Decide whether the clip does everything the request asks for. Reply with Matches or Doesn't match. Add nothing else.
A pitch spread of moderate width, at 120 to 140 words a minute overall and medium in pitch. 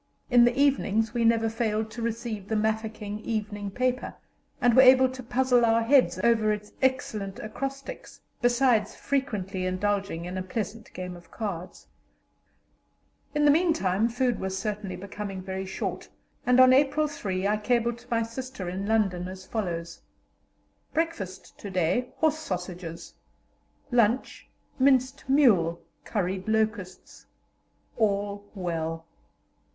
Doesn't match